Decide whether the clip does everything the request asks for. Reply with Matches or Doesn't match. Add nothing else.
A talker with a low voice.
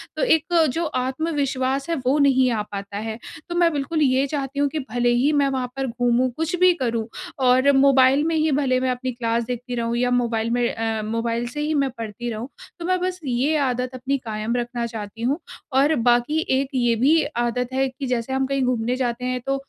Doesn't match